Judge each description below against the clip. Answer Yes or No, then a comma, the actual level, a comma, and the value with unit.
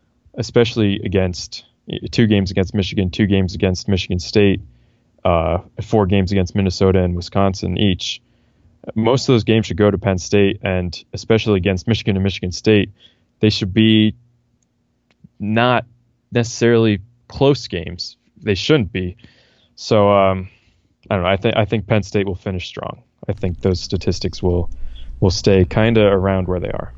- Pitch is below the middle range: Yes, low, 100 Hz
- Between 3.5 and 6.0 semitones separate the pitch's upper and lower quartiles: No, average, 3.1 semitones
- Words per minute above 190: No, average, 160 wpm